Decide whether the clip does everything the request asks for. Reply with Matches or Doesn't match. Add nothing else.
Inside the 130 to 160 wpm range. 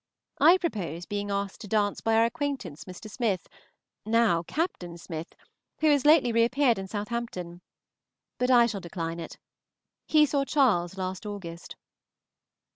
Matches